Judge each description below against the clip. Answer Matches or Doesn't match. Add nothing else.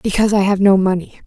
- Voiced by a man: Doesn't match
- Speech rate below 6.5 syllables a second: Doesn't match